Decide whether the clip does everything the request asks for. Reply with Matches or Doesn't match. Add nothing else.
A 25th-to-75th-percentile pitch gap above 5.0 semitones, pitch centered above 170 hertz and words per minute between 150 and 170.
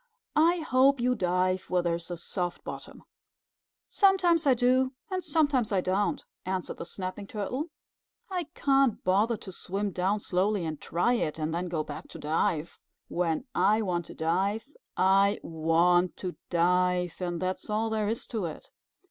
Matches